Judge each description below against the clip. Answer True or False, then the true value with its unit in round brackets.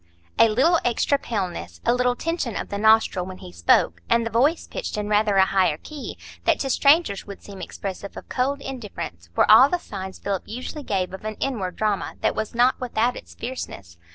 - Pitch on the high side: True (215 Hz)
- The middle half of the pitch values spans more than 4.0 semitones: True (5.0 semitones)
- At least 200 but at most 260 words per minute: True (205 wpm)